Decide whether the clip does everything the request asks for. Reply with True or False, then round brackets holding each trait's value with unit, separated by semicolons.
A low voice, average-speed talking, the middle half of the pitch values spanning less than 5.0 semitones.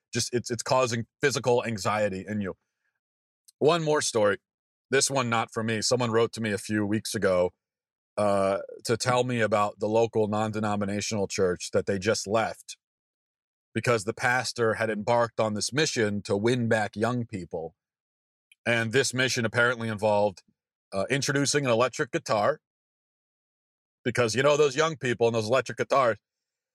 True (115 Hz; 155 wpm; 3.0 semitones)